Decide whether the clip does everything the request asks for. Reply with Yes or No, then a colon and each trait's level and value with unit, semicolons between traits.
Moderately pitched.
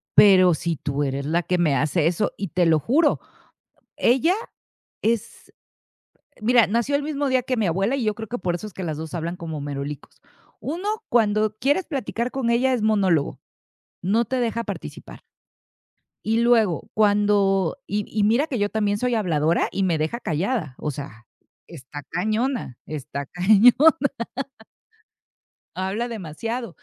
No: high, 205 Hz